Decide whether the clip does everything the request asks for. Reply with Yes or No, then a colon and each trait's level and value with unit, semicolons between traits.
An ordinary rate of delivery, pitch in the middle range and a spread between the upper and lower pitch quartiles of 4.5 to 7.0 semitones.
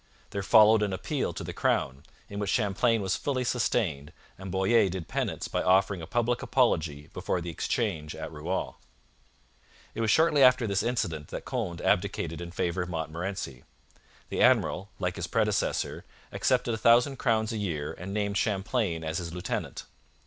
No: average, 170 wpm; very low, 95 Hz; average, 4.9 semitones